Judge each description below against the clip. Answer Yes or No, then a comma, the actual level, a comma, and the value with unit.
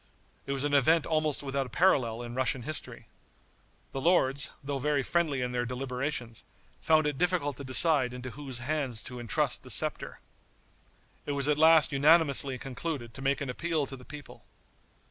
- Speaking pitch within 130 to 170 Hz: Yes, medium, 140 Hz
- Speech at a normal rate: Yes, average, 175 wpm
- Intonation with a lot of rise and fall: No, average, 3.2 semitones